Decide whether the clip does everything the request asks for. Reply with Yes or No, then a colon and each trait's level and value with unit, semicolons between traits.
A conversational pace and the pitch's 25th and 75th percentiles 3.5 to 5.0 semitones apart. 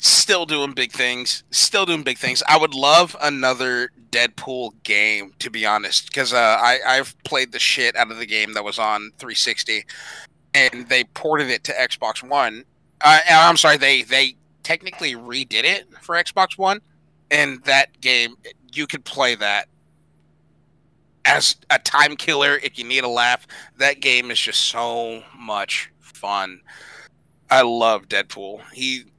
Yes: average, 160 wpm; average, 4.3 semitones